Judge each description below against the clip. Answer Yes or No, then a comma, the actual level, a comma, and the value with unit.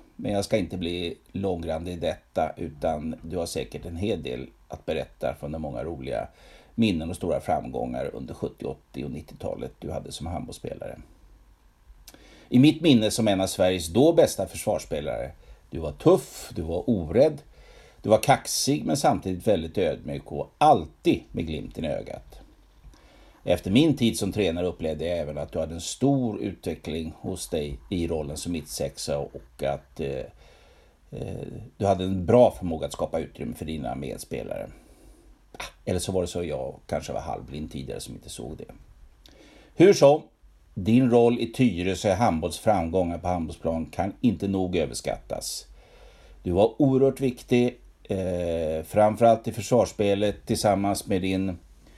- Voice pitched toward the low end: Yes, very low, 95 Hz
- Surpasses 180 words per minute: No, average, 160 wpm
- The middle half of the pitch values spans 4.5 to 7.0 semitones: Yes, average, 5.0 semitones